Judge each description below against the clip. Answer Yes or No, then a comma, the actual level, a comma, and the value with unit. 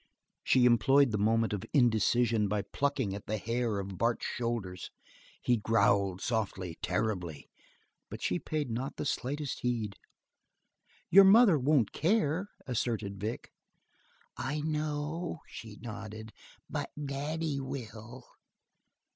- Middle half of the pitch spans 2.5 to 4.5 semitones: No, average, 5.1 semitones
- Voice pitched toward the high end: No, low, 120 Hz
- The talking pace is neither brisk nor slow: No, slow, 120 wpm